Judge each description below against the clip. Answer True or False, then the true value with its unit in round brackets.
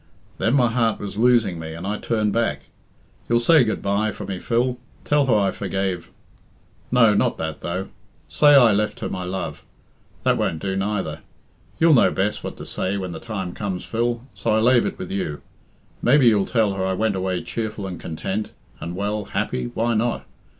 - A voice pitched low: True (105 Hz)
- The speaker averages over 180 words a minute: True (195 wpm)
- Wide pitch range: False (3.6 semitones)